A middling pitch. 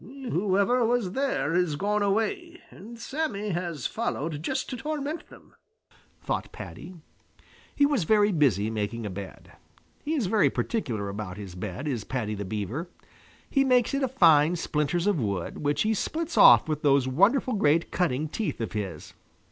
Yes: medium, 175 Hz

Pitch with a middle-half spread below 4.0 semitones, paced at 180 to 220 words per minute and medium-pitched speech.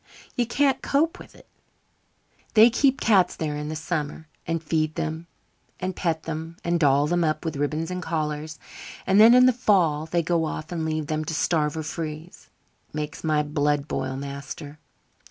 Yes: narrow, 2.6 semitones; average, 185 wpm; medium, 160 Hz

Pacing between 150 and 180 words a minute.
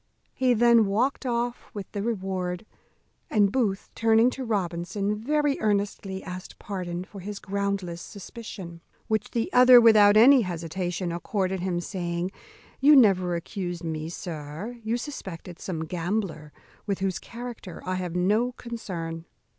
No: average, 140 wpm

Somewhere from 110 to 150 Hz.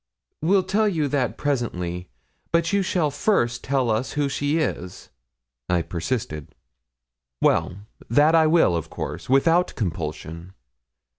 Yes: low, 135 Hz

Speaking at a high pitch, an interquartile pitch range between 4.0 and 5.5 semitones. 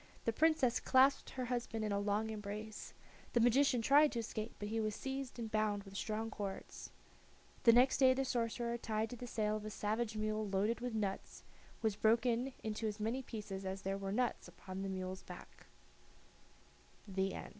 No: high, 220 Hz; average, 2.7 semitones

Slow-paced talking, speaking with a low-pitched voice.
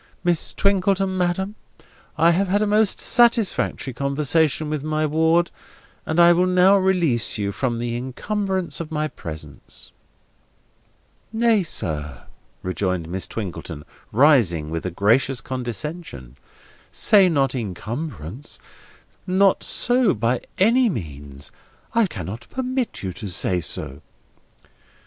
No: slow, 120 wpm; medium, 150 Hz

